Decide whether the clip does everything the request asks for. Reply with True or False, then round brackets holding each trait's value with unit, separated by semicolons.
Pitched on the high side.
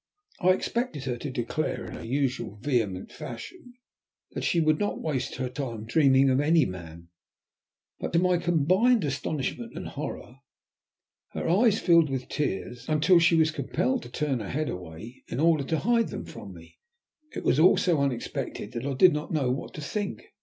False (145 Hz)